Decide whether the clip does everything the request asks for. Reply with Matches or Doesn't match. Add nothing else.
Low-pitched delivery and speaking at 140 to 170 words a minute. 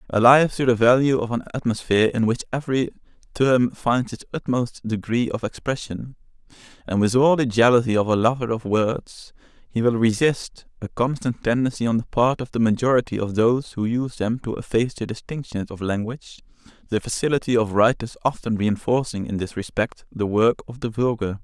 Doesn't match